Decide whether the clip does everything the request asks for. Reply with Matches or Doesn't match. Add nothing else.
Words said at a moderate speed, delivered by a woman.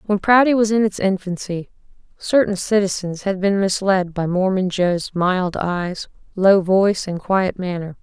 Matches